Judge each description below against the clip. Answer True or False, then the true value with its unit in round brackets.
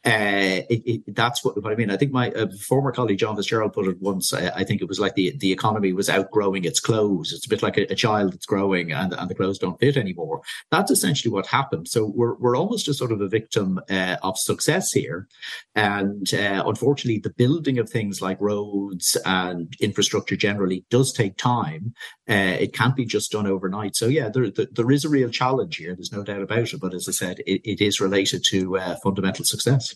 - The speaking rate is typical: False (230 wpm)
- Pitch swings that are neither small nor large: True (3.8 semitones)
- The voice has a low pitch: True (105 Hz)